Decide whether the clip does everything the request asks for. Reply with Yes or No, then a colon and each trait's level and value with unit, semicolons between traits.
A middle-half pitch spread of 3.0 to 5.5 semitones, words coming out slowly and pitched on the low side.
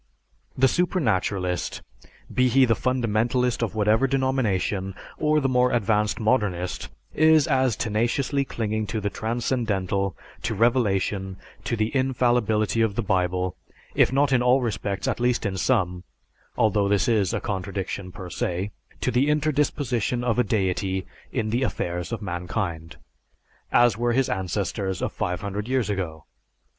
No: average, 4.5 semitones; average, 145 wpm; low, 110 Hz